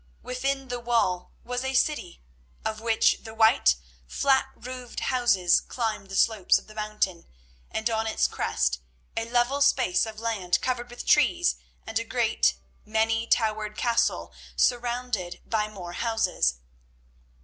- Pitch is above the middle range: Yes, high, 225 Hz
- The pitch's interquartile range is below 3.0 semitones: Yes, narrow, 2.6 semitones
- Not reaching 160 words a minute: Yes, average, 140 wpm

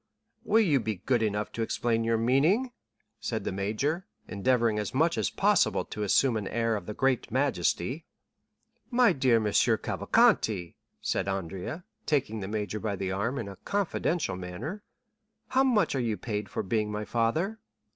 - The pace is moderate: Yes, average, 165 wpm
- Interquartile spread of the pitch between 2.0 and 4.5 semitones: No, wide, 5.6 semitones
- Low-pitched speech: Yes, low, 115 Hz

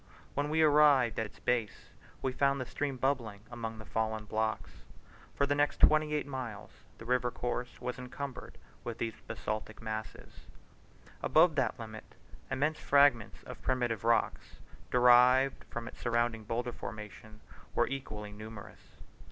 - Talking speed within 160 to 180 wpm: No, average, 145 wpm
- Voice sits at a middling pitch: No, low, 120 Hz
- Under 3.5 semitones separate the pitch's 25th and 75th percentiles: No, average, 3.8 semitones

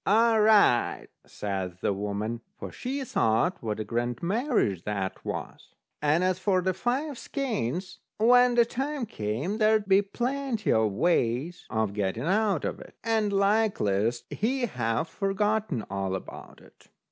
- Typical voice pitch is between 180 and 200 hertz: Yes, medium, 185 Hz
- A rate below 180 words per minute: Yes, average, 145 wpm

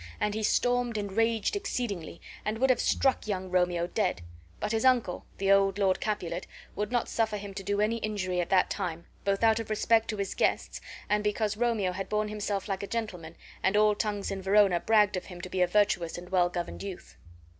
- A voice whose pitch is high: Yes, high, 205 Hz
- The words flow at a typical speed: No, fast, 215 wpm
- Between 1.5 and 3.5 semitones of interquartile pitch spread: Yes, average, 2.8 semitones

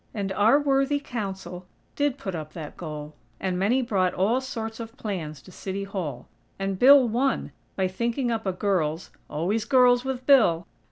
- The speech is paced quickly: No, average, 170 wpm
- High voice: Yes, high, 200 Hz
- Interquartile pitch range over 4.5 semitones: Yes, wide, 5.4 semitones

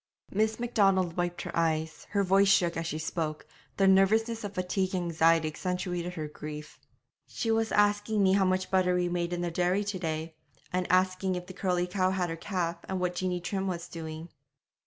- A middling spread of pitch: No, narrow, 2.3 semitones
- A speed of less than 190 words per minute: No, average, 200 wpm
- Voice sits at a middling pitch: Yes, medium, 180 Hz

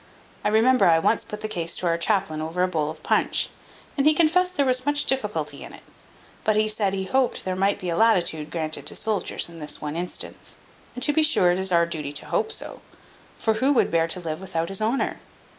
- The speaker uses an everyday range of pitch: No, wide, 6.6 semitones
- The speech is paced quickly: Yes, fast, 235 wpm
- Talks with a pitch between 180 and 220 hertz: Yes, high, 190 Hz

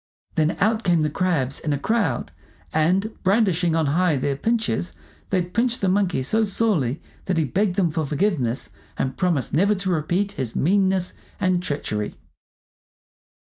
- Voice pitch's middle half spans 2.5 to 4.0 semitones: No, average, 4.7 semitones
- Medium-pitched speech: Yes, medium, 180 Hz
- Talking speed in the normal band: Yes, average, 155 wpm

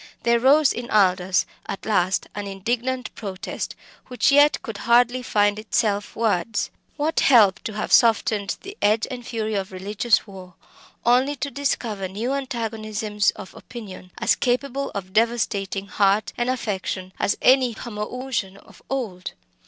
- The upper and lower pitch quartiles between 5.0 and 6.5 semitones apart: No, average, 3.8 semitones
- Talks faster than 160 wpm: No, average, 145 wpm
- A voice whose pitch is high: Yes, high, 220 Hz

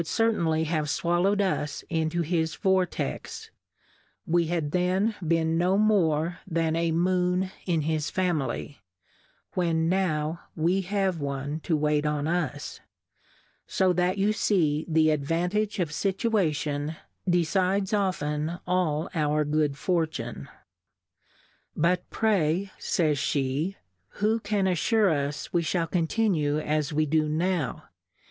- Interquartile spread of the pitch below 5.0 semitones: Yes, average, 3.4 semitones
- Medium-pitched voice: Yes, medium, 165 Hz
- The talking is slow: Yes, slow, 125 wpm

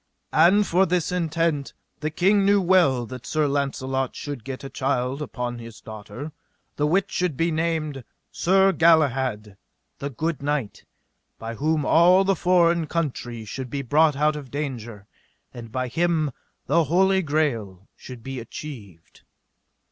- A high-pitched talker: No, medium, 145 Hz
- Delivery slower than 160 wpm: Yes, average, 150 wpm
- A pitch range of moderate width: Yes, average, 5.0 semitones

